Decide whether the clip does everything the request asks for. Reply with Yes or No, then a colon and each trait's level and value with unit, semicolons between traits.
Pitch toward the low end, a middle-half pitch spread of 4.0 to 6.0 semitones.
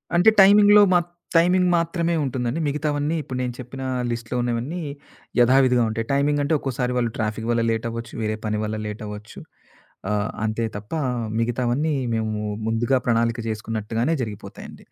Yes: low, 120 Hz; average, 4.6 semitones